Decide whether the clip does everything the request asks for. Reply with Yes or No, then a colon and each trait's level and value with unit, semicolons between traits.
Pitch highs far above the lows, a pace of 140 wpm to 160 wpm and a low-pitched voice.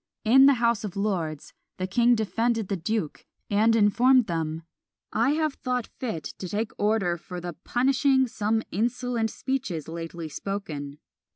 No: wide, 5.7 semitones; average, 150 wpm; high, 215 Hz